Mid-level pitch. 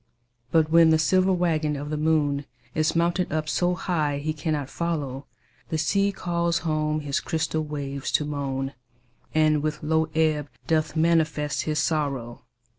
Yes: medium, 155 Hz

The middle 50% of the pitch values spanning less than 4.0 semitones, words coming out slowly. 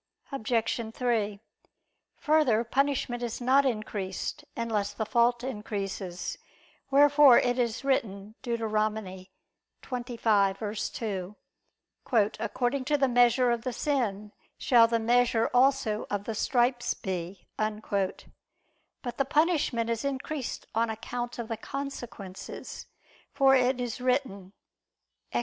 Yes: average, 3.3 semitones; slow, 110 wpm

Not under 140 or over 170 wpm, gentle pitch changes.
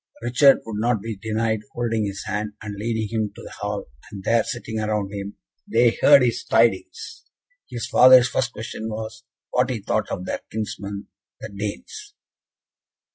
Yes: average, 165 wpm; narrow, 2.2 semitones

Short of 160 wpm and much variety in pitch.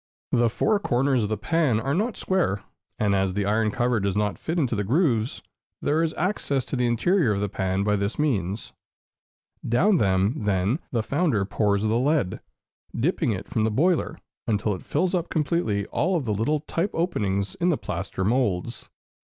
No: average, 185 wpm; wide, 7.6 semitones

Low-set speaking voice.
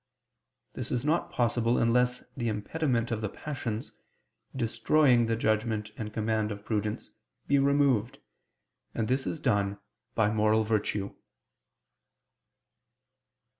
Yes: low, 115 Hz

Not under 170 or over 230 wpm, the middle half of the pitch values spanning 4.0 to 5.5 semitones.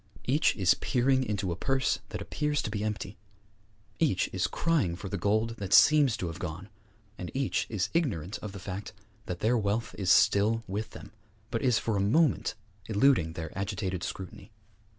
Yes: average, 180 wpm; average, 4.6 semitones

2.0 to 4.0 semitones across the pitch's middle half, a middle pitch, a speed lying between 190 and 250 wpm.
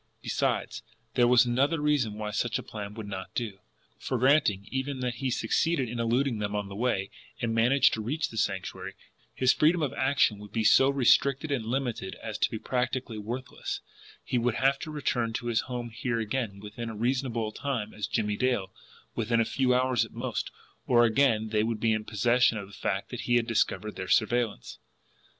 No: average, 3.2 semitones; low, 120 Hz; average, 200 wpm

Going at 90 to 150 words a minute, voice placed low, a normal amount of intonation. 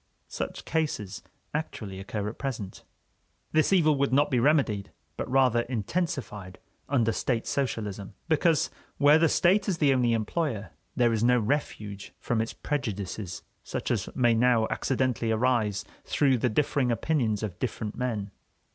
Yes: average, 145 wpm; low, 120 Hz; average, 5.0 semitones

